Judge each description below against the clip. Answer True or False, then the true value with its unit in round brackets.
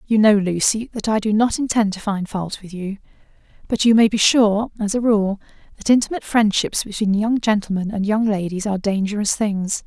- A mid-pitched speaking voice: False (210 Hz)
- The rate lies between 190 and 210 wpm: True (200 wpm)